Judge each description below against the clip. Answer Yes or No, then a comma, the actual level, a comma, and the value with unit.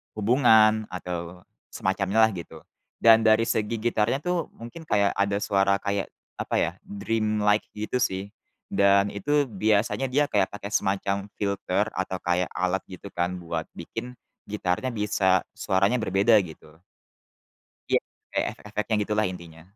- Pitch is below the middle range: Yes, low, 100 Hz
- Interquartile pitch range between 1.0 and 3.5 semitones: Yes, average, 2.8 semitones